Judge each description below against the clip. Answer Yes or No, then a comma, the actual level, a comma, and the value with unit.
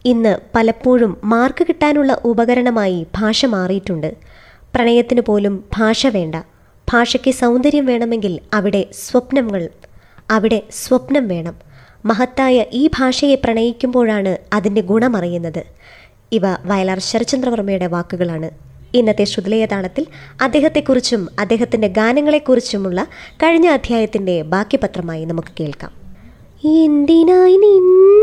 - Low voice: No, high, 230 Hz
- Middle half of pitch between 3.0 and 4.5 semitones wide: No, average, 5.1 semitones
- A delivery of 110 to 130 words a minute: No, average, 85 wpm